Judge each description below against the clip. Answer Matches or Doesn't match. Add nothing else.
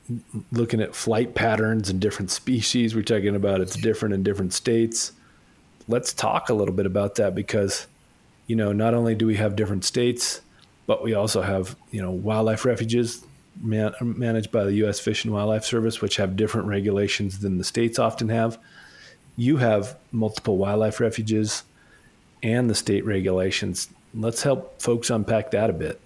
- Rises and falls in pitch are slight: Matches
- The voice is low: Matches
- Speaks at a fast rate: Doesn't match